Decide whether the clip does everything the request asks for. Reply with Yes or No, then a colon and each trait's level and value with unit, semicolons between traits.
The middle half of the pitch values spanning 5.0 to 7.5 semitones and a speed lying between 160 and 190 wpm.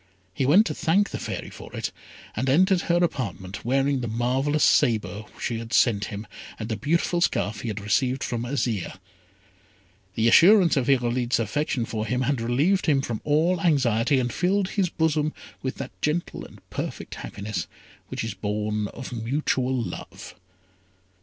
Yes: average, 5.3 semitones; average, 165 wpm